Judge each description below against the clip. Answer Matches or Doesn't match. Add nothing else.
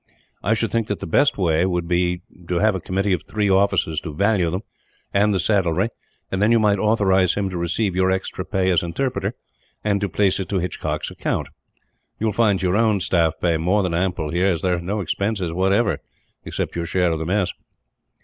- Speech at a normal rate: Doesn't match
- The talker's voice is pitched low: Matches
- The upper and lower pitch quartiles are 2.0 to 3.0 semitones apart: Matches